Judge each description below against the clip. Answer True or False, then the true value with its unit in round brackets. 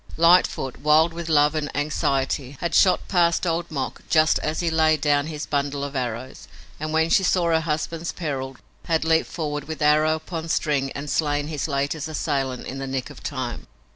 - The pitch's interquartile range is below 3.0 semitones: True (2.4 semitones)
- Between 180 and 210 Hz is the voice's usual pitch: False (150 Hz)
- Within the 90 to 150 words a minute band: False (190 wpm)